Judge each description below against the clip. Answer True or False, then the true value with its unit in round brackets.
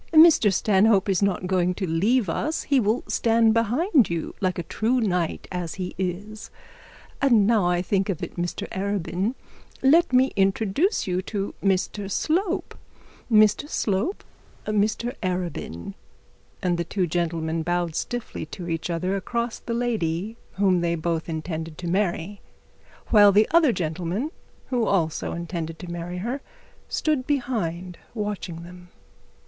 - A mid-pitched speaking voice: False (195 Hz)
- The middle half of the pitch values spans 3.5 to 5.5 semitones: True (4.7 semitones)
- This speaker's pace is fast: False (140 wpm)